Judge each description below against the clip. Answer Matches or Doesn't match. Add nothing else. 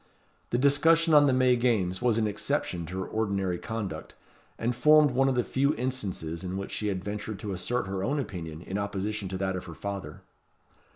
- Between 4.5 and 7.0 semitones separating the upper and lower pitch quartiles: Matches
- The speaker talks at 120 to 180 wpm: Doesn't match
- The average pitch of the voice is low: Matches